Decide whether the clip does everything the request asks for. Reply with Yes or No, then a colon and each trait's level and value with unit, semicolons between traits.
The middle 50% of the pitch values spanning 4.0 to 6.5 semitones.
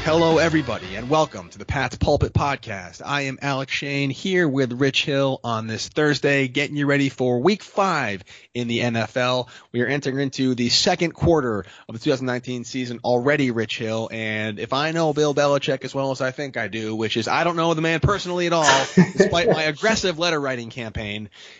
Yes: average, 4.6 semitones